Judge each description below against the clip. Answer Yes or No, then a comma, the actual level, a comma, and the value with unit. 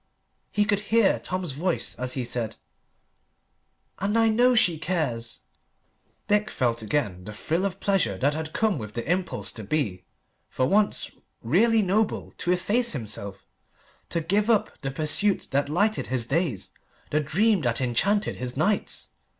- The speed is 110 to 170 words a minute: Yes, average, 155 wpm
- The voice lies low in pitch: No, medium, 160 Hz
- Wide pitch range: Yes, wide, 8.8 semitones